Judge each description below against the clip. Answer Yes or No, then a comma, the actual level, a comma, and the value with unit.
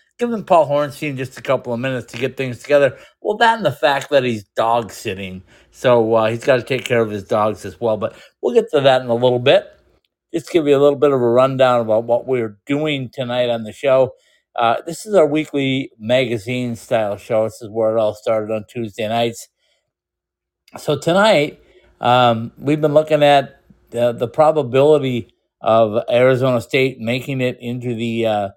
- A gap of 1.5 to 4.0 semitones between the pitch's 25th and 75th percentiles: Yes, average, 3.3 semitones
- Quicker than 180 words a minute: Yes, average, 200 wpm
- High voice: No, low, 125 Hz